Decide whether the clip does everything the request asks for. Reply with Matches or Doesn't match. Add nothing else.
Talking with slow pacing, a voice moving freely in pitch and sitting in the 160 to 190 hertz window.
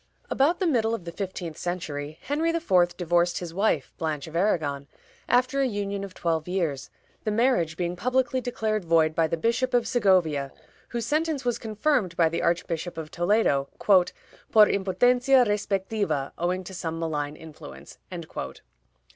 Doesn't match